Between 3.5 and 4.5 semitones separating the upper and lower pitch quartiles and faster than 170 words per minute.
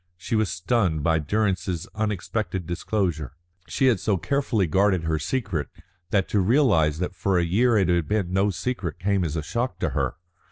Yes: average, 4.2 semitones; average, 185 wpm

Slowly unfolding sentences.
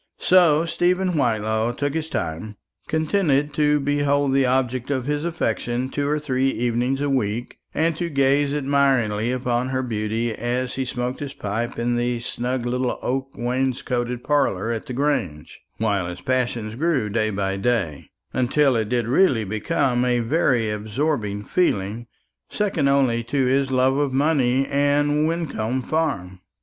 No: average, 155 wpm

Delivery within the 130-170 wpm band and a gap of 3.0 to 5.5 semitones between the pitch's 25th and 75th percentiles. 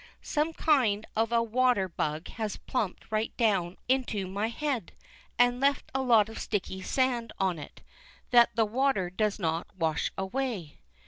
Yes: average, 155 wpm; average, 4.9 semitones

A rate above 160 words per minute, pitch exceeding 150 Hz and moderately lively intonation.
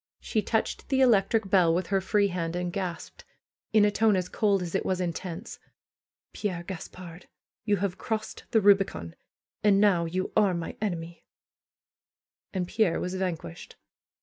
No: average, 155 wpm; high, 190 Hz; average, 3.0 semitones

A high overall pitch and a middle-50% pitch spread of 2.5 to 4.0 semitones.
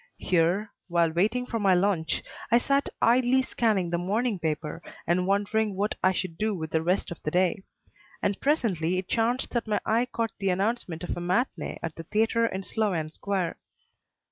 No: high, 195 Hz; average, 4.5 semitones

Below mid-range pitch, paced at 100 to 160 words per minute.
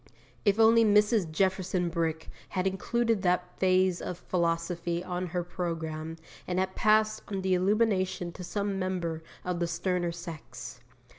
No: medium, 180 Hz; average, 145 wpm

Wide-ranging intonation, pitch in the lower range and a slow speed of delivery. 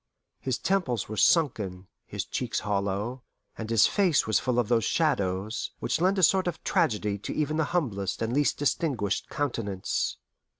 No: wide, 7.2 semitones; low, 120 Hz; average, 165 wpm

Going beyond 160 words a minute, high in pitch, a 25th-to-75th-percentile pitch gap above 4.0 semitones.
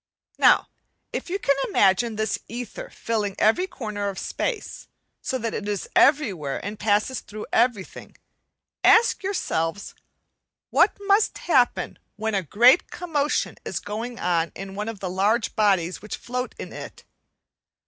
No: average, 145 wpm; high, 215 Hz; average, 4.4 semitones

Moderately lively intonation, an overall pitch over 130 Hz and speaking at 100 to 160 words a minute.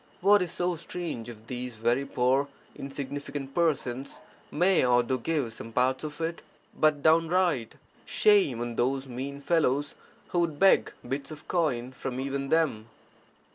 Yes: average, 4.5 semitones; medium, 140 Hz; average, 150 wpm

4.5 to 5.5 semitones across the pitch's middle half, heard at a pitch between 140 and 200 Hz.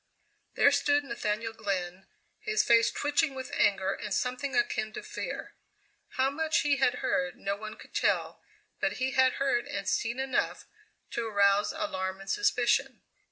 No: average, 5.1 semitones; very high, 250 Hz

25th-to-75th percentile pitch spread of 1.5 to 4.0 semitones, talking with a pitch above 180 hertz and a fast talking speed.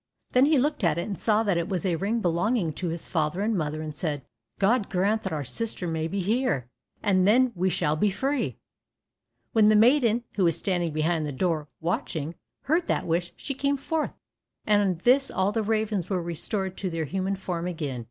No: average, 4.9 semitones; high, 190 Hz; fast, 210 wpm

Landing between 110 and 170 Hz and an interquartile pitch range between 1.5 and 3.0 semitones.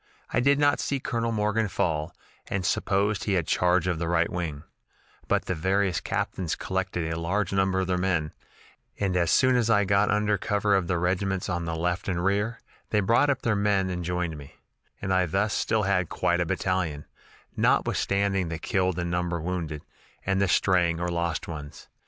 No: very low, 95 Hz; average, 2.7 semitones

